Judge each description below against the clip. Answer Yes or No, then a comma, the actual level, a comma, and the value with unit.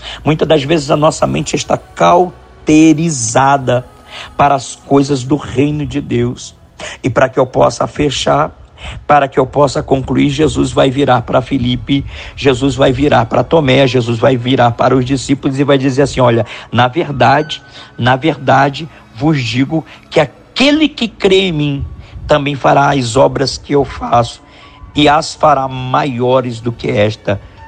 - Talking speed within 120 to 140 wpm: No, average, 160 wpm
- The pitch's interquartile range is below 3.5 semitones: Yes, average, 3.0 semitones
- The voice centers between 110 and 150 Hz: Yes, medium, 140 Hz